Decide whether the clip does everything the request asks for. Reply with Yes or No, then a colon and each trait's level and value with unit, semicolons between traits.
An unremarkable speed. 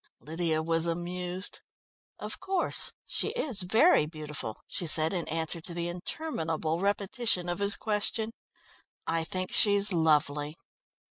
No: slow, 130 wpm